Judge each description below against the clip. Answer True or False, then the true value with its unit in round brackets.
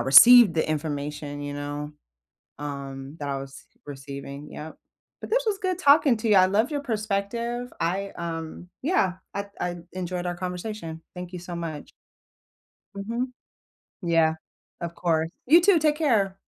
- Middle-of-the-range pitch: True (180 Hz)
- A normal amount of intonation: False (7.5 semitones)